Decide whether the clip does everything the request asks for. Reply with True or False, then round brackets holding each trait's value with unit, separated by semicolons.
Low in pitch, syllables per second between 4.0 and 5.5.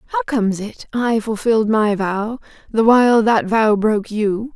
False (220 Hz; 4.6 syllables/s)